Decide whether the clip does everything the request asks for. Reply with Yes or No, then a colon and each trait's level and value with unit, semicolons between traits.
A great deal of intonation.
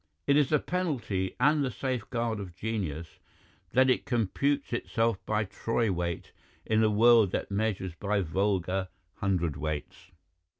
No: average, 4.4 semitones